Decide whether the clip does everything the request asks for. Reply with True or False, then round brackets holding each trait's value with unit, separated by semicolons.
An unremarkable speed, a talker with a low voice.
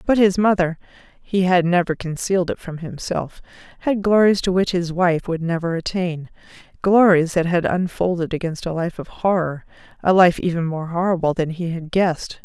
False (165 wpm; 175 Hz)